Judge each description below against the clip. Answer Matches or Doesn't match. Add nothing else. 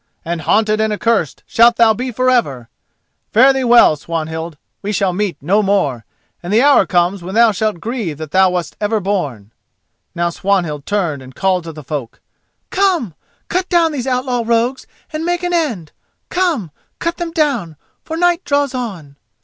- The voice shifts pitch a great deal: Matches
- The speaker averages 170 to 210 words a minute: Matches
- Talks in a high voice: Matches